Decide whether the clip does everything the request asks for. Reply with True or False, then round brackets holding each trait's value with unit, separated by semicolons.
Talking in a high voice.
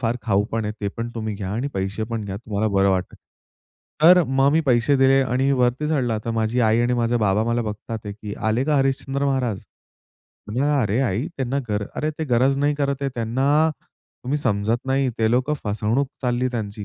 False (120 Hz)